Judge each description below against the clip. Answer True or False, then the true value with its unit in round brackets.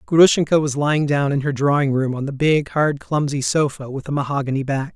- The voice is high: False (140 Hz)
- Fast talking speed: True (220 wpm)